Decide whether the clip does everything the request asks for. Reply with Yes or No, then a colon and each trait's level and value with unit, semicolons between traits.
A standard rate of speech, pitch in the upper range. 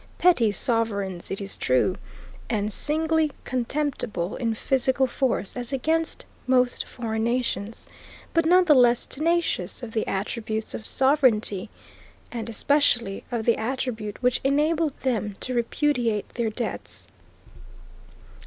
No: slow, 125 wpm; high, 240 Hz